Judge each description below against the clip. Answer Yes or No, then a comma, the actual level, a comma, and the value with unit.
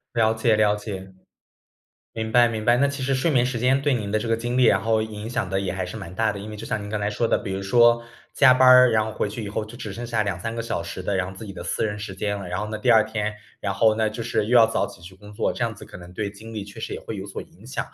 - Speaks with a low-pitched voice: Yes, low, 110 Hz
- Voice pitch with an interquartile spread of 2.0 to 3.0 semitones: Yes, narrow, 2.4 semitones